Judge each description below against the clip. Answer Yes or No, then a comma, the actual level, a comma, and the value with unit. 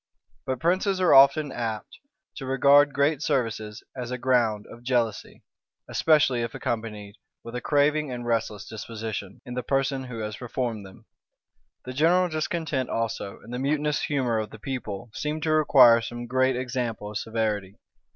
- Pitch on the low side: Yes, low, 125 Hz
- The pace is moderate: Yes, average, 160 wpm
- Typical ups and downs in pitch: Yes, average, 4.1 semitones